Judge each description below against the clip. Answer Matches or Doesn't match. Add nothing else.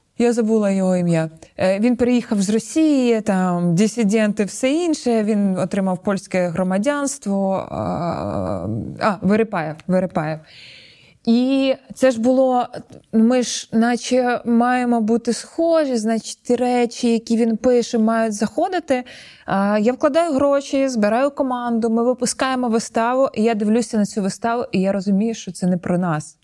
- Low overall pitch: Doesn't match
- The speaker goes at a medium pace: Matches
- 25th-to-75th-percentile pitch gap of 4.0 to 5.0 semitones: Matches